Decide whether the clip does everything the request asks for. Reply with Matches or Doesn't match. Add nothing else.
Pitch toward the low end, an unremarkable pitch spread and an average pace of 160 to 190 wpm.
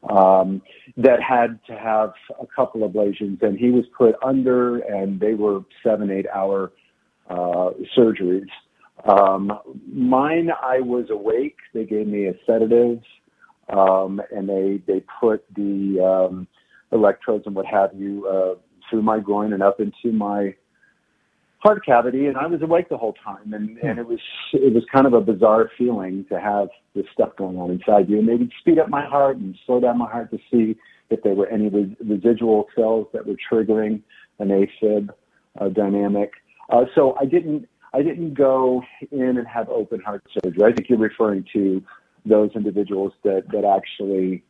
Matches